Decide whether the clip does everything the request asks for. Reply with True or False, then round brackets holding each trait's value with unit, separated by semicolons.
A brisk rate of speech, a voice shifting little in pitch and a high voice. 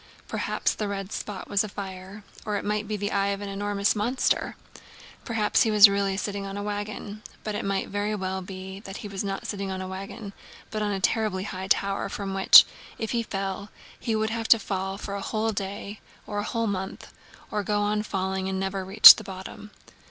True (215 wpm; 1.5 semitones; 200 Hz)